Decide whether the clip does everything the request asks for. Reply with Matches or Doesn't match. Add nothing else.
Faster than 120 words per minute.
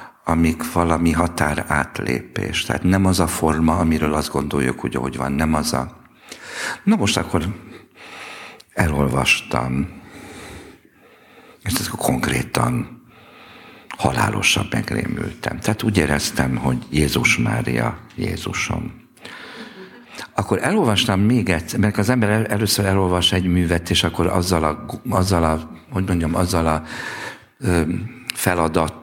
Doesn't match